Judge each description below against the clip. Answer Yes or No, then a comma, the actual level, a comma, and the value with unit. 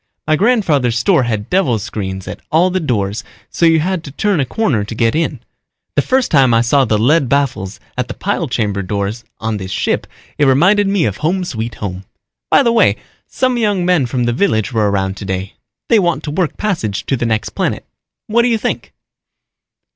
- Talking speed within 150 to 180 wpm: No, fast, 205 wpm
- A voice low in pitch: Yes, low, 130 Hz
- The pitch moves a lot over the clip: Yes, wide, 8.9 semitones